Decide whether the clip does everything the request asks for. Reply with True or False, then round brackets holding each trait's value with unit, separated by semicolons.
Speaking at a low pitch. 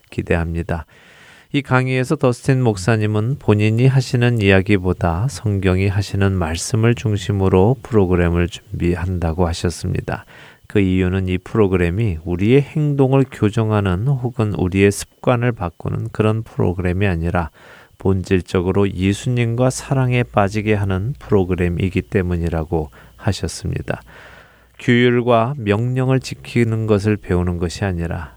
True (105 Hz)